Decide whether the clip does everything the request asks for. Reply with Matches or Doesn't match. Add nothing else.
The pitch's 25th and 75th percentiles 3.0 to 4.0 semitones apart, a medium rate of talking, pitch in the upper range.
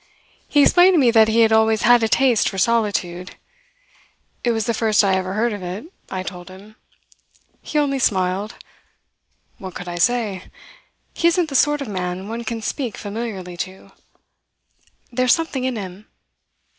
Doesn't match